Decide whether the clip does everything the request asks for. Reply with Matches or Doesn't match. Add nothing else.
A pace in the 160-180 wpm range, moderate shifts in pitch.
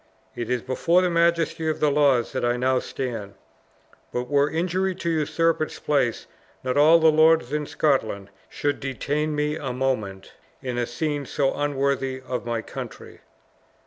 Matches